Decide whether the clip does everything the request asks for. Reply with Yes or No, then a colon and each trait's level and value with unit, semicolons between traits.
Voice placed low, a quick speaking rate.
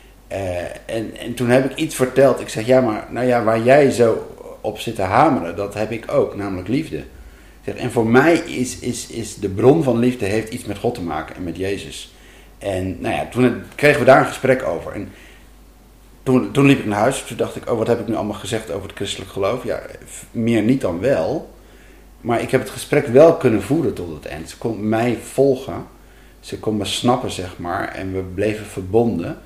Yes: low, 115 Hz; fast, 220 wpm